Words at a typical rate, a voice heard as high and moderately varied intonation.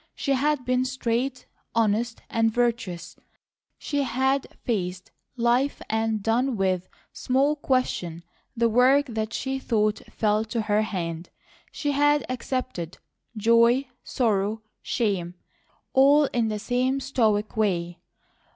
No: slow, 120 wpm; high, 230 Hz; average, 3.7 semitones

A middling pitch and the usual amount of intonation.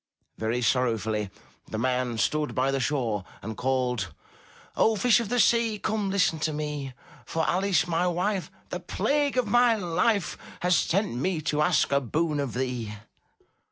No: medium, 150 Hz; wide, 8.0 semitones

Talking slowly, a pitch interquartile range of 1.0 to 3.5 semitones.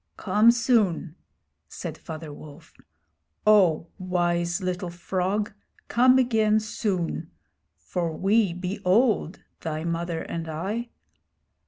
No: slow, 105 wpm; average, 4.1 semitones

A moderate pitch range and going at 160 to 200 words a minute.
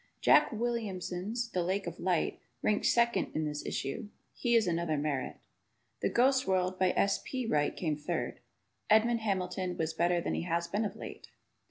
Yes: average, 4.6 semitones; average, 175 wpm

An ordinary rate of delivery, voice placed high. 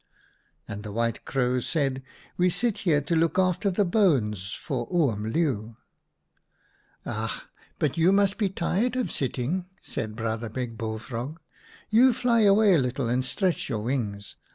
No: average, 180 wpm; medium, 140 Hz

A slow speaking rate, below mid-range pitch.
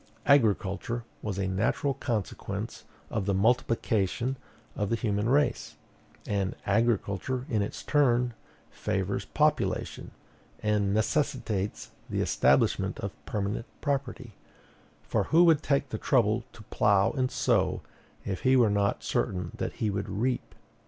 Yes: slow, 130 wpm; low, 110 Hz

